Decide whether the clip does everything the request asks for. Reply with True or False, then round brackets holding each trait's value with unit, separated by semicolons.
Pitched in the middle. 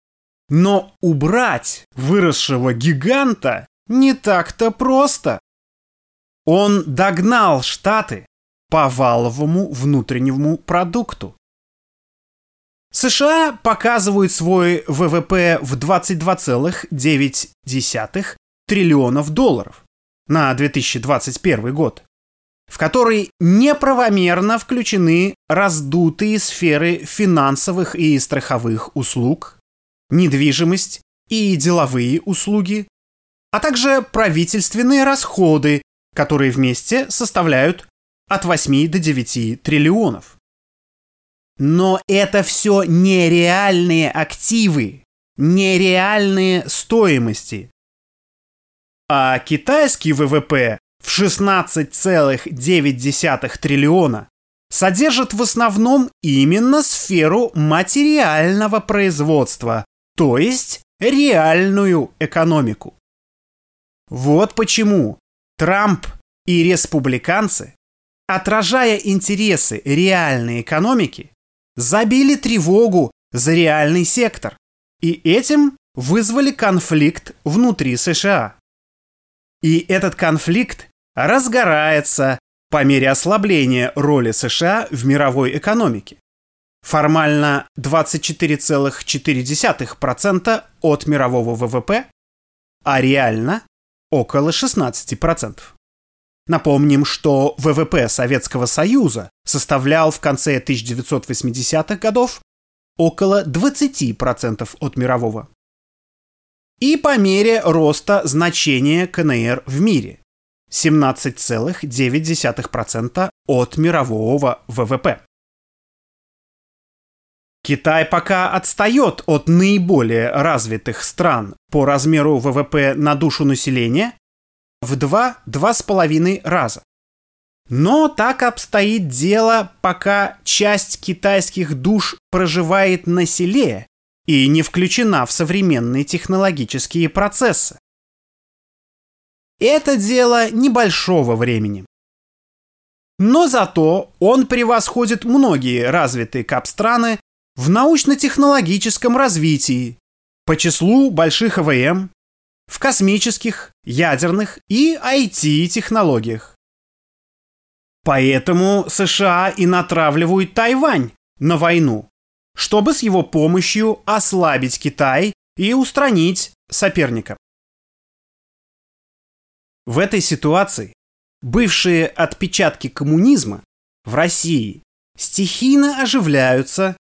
True (165 Hz)